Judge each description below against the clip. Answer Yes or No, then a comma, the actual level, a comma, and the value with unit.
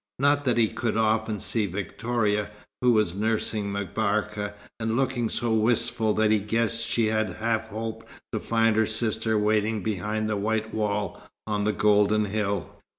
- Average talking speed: Yes, average, 160 wpm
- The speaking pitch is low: Yes, low, 110 Hz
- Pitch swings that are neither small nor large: No, narrow, 1.3 semitones